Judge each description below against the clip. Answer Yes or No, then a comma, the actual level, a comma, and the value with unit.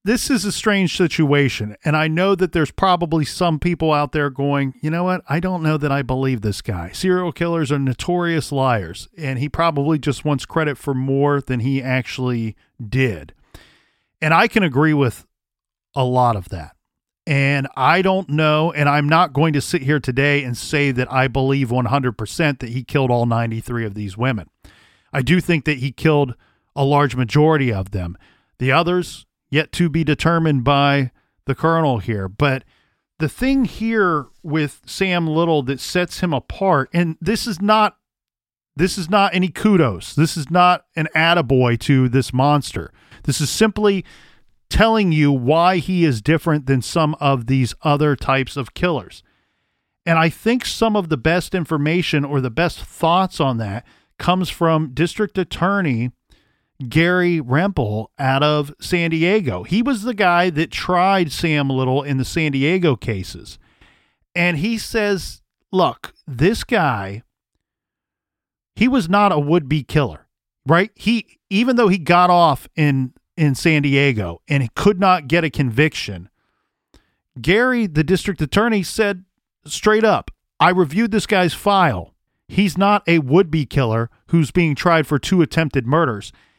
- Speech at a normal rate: Yes, average, 165 wpm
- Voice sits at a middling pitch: Yes, medium, 150 Hz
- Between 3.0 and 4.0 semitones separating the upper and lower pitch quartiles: No, average, 5.2 semitones